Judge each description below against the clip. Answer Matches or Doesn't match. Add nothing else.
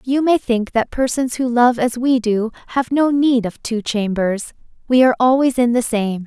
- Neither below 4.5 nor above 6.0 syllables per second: Matches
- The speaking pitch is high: Matches